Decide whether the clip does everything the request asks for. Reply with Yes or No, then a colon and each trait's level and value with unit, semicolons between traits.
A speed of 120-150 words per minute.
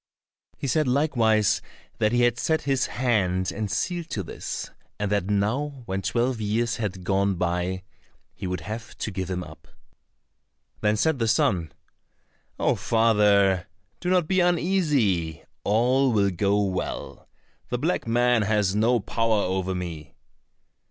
Yes: average, 145 wpm